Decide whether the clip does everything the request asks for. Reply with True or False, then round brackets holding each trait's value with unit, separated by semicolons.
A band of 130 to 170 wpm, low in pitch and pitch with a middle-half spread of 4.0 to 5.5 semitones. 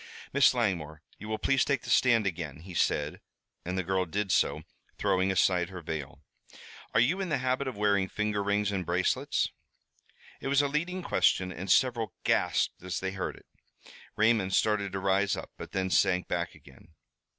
False (185 wpm; 100 Hz; 4.3 semitones)